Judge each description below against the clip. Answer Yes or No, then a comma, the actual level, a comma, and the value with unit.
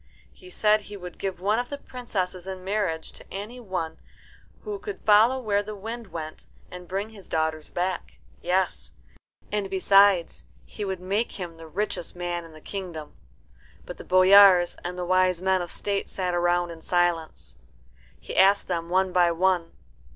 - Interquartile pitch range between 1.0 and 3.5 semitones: Yes, narrow, 2.6 semitones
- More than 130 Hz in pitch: Yes, medium, 185 Hz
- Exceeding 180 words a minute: No, average, 175 wpm